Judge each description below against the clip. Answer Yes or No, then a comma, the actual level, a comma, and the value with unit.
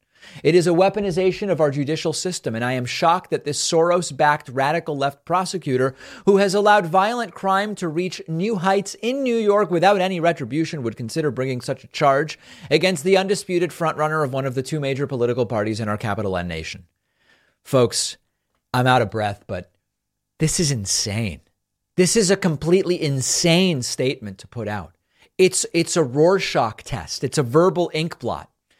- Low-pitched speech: No, medium, 155 Hz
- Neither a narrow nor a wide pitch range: No, wide, 6.8 semitones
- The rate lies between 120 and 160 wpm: No, average, 175 wpm